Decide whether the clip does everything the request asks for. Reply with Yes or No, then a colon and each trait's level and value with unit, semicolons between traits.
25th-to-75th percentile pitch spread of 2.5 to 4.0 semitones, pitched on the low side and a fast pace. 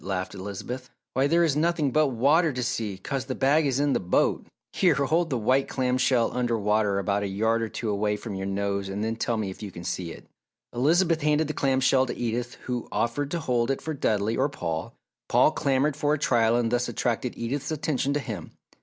No: average, 5.0 semitones; low, 125 Hz; fast, 225 wpm